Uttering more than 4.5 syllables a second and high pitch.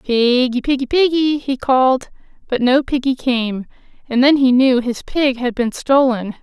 No: 4.4 syllables/s; very high, 260 Hz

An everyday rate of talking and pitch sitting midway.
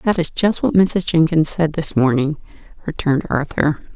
Yes: average, 165 wpm; medium, 160 Hz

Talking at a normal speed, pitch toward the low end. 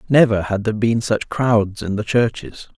Yes: average, 195 wpm; low, 110 Hz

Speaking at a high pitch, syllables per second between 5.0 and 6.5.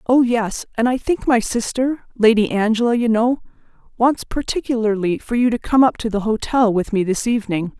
Yes: high, 230 Hz; 5.2 syllables/s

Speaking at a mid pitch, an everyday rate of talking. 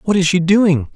No: medium, 180 Hz; fast, 250 wpm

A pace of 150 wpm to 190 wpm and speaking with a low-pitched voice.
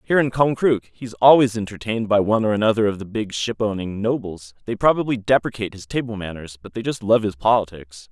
No: fast, 205 wpm; low, 105 Hz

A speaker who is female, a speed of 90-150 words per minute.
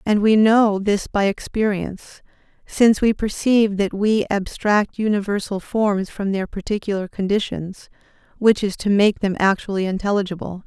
Yes: female; average, 140 wpm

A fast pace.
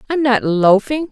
No: average, 160 wpm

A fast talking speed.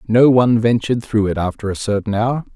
Yes: fast, 210 wpm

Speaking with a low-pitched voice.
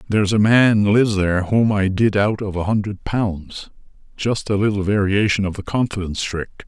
Yes: low, 100 Hz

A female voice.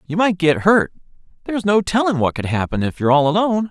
No: male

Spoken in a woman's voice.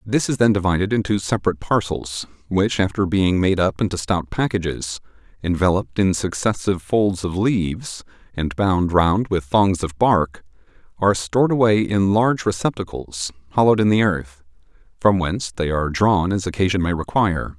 No: male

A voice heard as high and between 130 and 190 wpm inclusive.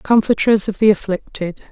Yes: high, 205 Hz; average, 140 wpm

